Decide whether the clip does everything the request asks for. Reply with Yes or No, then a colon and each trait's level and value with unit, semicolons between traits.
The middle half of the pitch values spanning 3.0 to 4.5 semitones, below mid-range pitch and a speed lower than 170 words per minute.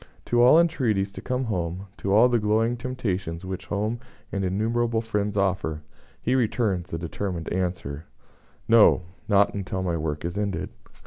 Yes: average, 4.1 semitones; low, 100 Hz; average, 155 wpm